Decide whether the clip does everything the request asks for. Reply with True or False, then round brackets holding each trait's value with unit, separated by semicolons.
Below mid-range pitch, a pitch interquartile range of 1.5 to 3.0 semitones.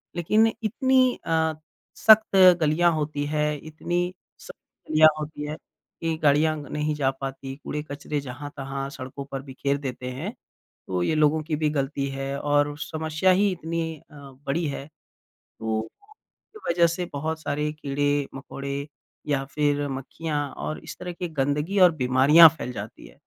False (150 Hz; 2.7 semitones)